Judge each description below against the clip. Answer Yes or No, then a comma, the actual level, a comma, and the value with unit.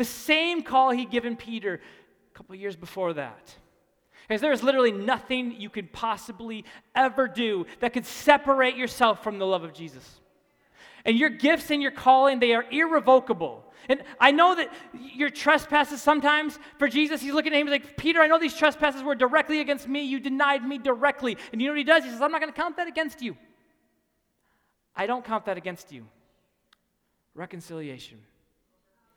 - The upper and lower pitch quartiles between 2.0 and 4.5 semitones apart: No, average, 5.0 semitones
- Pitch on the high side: Yes, very high, 260 Hz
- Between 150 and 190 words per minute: Yes, average, 185 wpm